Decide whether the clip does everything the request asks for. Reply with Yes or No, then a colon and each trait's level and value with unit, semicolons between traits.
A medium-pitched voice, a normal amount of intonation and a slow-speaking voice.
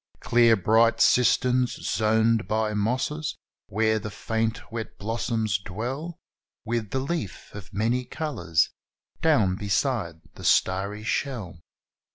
No: low, 110 Hz; average, 3.5 semitones; slow, 115 wpm